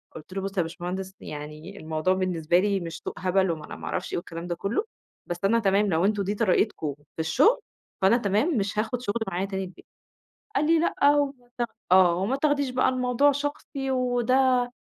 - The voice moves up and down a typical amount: No, wide, 6.2 semitones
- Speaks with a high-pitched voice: Yes, high, 200 Hz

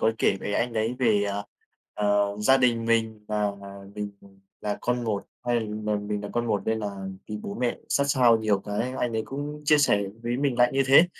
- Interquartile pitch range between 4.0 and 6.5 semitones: No, average, 3.0 semitones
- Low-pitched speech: Yes, low, 110 Hz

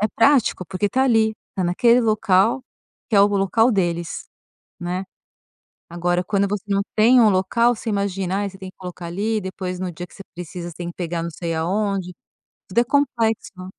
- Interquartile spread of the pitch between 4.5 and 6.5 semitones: No, average, 3.5 semitones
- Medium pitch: No, high, 195 Hz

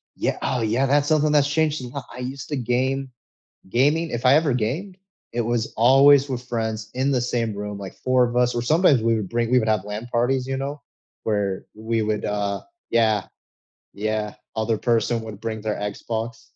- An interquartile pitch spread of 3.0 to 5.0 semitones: Yes, average, 3.5 semitones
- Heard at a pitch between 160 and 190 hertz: No, low, 120 Hz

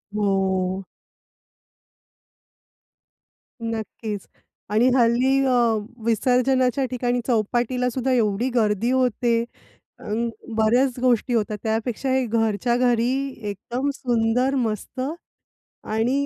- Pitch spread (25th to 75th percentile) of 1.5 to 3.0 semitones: Yes, narrow, 2.5 semitones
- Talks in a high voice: Yes, high, 235 Hz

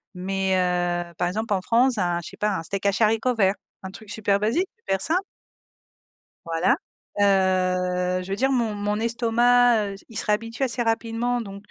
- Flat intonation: No, average, 3.6 semitones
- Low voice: No, high, 205 Hz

